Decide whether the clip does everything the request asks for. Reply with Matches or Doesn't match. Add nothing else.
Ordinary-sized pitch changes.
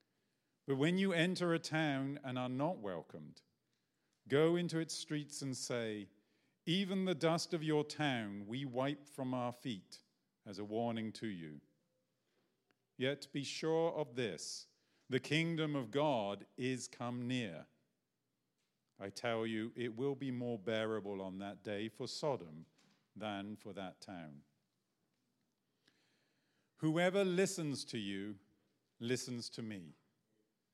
Doesn't match